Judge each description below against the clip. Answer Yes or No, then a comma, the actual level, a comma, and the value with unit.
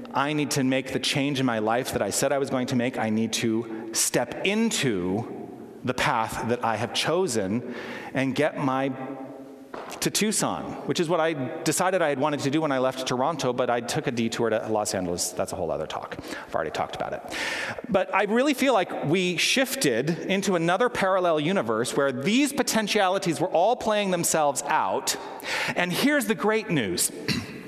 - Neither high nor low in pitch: Yes, medium, 150 Hz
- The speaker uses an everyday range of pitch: No, wide, 6.8 semitones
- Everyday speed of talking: Yes, average, 195 wpm